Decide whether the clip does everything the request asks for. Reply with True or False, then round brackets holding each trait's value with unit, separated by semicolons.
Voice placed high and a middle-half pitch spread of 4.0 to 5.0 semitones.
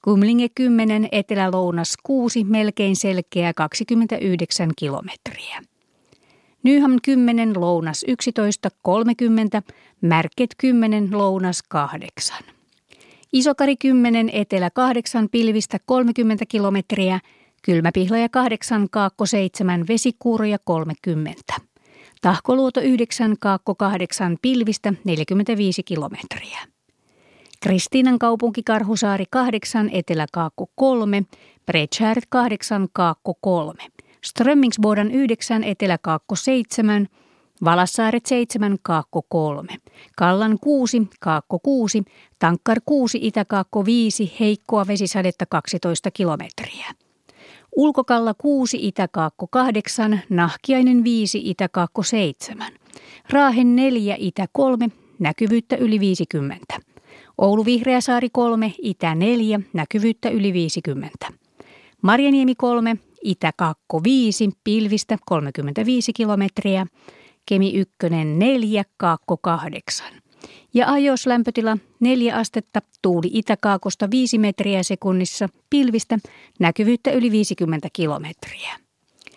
True (210 Hz; 4.3 semitones)